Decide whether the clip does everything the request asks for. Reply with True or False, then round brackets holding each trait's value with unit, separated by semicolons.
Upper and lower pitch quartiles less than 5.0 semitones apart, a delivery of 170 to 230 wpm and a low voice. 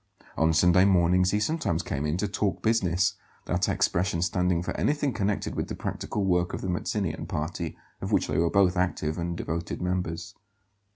True (2.4 semitones; 180 wpm; 90 Hz)